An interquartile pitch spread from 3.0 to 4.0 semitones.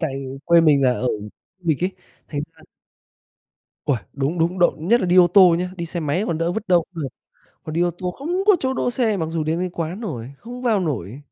Yes: average, 3.4 semitones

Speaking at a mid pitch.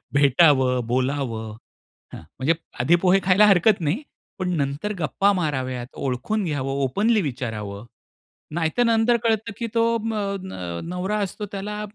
Yes: medium, 165 Hz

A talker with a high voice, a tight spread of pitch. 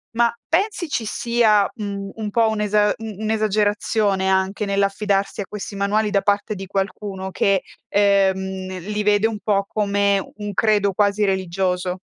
Yes: high, 205 Hz; narrow, 1.5 semitones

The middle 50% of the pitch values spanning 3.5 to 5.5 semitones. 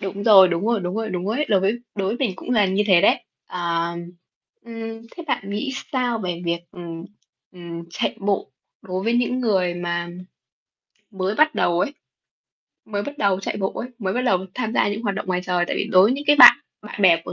Yes: average, 4.1 semitones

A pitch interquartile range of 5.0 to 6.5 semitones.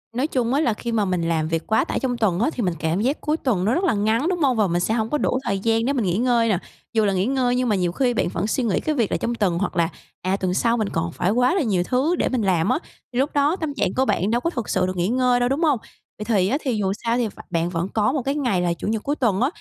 Yes: average, 5.3 semitones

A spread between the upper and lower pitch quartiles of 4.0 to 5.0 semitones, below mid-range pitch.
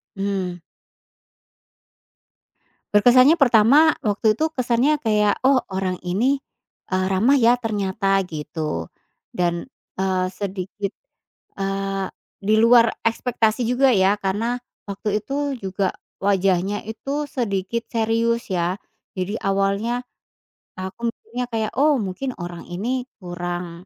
No: average, 4.3 semitones; high, 205 Hz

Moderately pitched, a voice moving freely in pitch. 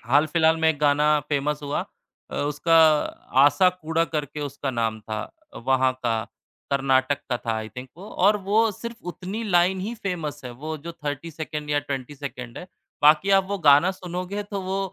No: medium, 150 Hz; average, 4.8 semitones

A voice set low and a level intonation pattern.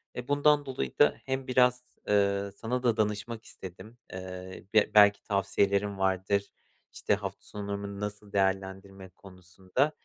No: low, 100 Hz; average, 3.0 semitones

